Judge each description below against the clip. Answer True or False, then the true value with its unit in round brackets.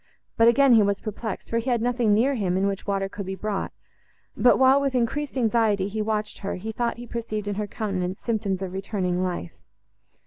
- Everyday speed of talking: False (210 wpm)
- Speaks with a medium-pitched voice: False (215 Hz)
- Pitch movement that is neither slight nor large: True (3.2 semitones)